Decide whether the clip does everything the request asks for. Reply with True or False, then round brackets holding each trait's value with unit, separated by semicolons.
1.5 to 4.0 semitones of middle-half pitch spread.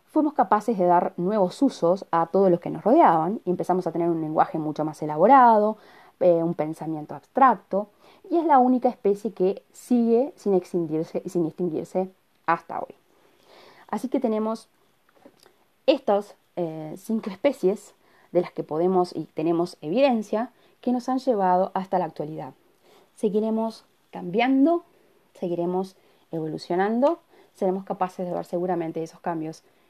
False (5.1 semitones)